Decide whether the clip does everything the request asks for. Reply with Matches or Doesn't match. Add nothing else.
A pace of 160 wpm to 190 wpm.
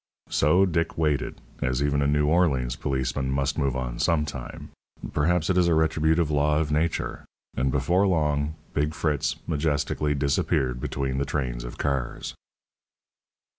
Doesn't match